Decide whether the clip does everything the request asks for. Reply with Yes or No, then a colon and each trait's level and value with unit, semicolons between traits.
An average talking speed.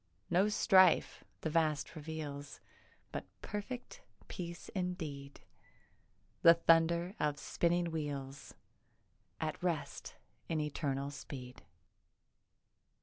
No: slow, 90 wpm